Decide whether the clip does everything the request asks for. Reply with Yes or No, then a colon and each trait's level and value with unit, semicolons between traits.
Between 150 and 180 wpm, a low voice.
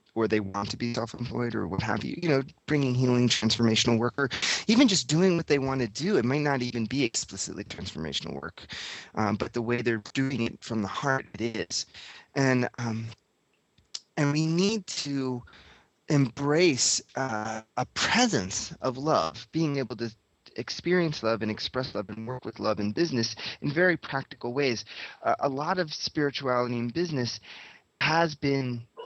Yes: average, 175 wpm; low, 125 Hz